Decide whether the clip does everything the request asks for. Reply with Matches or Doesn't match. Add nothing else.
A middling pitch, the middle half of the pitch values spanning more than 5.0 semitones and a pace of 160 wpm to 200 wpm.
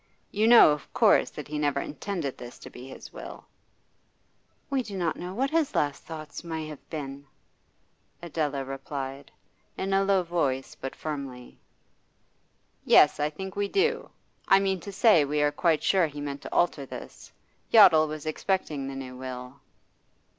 Matches